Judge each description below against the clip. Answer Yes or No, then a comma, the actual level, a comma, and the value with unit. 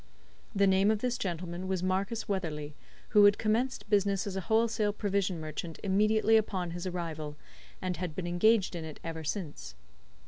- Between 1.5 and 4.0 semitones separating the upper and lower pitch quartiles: Yes, average, 3.5 semitones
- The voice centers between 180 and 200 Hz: Yes, high, 190 Hz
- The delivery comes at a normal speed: Yes, average, 170 wpm